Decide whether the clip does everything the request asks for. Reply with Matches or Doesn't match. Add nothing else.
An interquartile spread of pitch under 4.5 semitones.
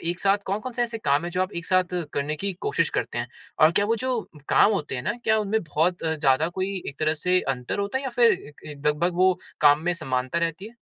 Doesn't match